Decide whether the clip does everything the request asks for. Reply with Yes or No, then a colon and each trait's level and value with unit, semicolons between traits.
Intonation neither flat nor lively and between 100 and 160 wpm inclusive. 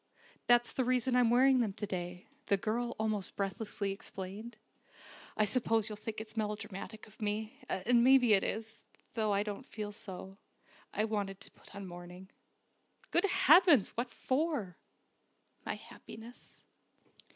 Yes: average, 3.3 semitones; average, 145 wpm